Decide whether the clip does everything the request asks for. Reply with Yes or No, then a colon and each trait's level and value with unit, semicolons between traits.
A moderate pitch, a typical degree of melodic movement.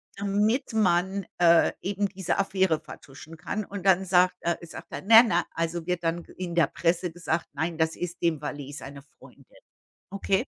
Yes: medium, 175 Hz; average, 3.0 semitones